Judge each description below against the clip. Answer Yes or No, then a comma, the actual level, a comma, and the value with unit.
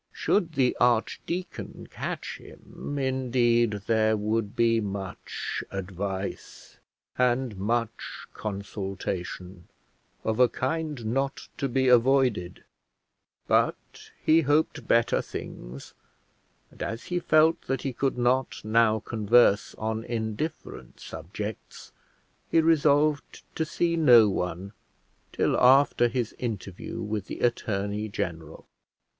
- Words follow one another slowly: Yes, slow, 110 wpm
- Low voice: Yes, low, 115 Hz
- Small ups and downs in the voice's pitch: No, average, 4.5 semitones